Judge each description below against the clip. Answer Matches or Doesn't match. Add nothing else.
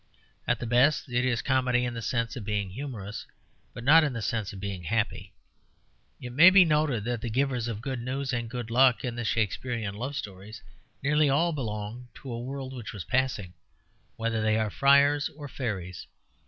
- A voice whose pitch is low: Matches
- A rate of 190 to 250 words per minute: Matches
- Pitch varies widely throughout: Doesn't match